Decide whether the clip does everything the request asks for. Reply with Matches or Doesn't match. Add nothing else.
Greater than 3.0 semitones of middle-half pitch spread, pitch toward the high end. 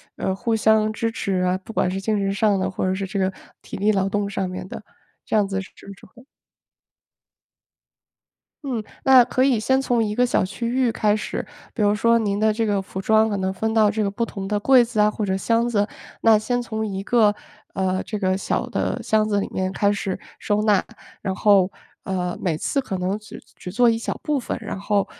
Doesn't match